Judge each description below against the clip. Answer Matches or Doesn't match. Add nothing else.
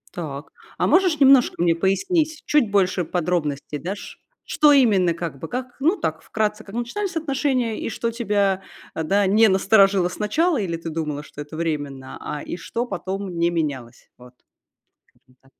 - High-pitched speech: Matches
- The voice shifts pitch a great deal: Matches